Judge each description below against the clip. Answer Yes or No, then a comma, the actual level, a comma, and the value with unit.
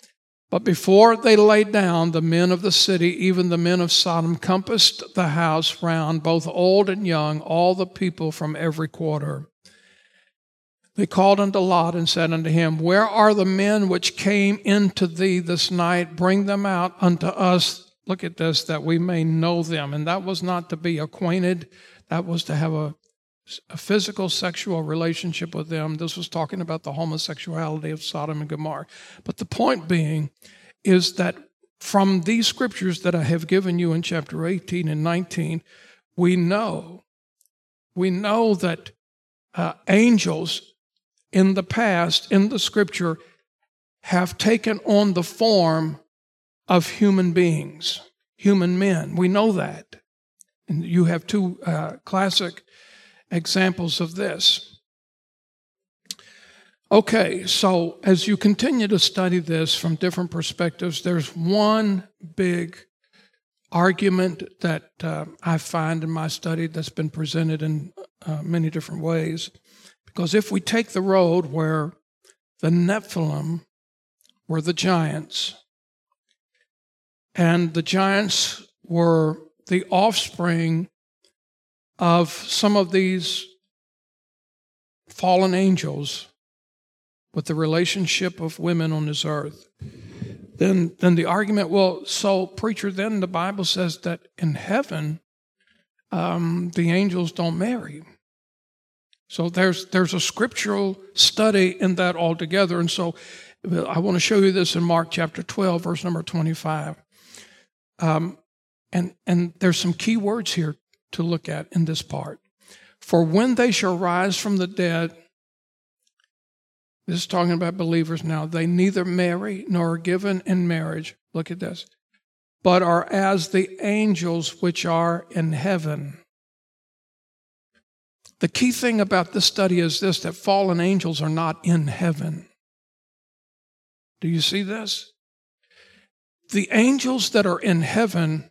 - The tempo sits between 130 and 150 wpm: Yes, average, 140 wpm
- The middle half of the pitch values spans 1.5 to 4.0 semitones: Yes, average, 2.7 semitones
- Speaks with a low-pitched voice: No, medium, 175 Hz